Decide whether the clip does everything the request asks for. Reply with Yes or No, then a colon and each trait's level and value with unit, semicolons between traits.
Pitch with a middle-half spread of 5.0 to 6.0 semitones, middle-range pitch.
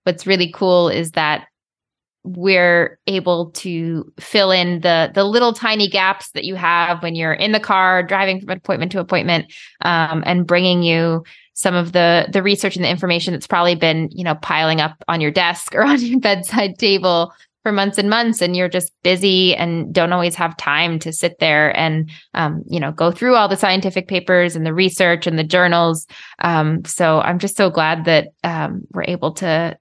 No: narrow, 2.4 semitones; medium, 175 Hz